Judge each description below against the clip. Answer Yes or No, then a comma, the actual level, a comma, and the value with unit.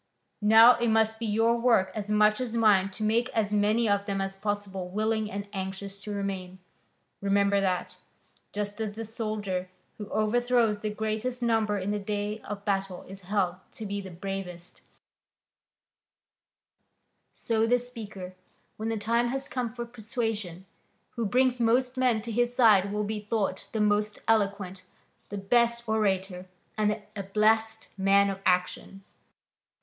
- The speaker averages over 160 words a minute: No, average, 155 wpm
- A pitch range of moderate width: No, narrow, 2.3 semitones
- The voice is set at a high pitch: Yes, high, 210 Hz